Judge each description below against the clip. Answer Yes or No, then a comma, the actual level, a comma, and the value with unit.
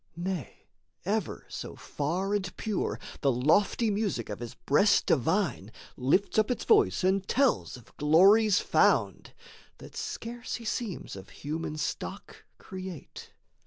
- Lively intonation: Yes, wide, 6.2 semitones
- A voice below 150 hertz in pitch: No, high, 190 Hz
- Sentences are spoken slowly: Yes, slow, 130 wpm